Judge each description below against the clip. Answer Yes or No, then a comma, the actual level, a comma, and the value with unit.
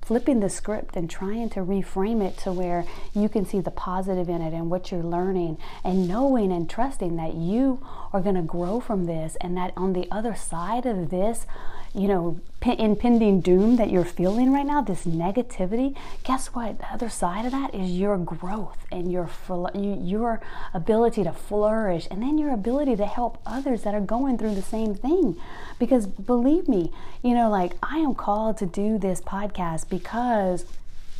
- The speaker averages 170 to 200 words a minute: Yes, average, 190 wpm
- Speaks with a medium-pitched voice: No, high, 200 Hz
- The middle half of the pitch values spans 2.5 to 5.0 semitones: Yes, average, 4.6 semitones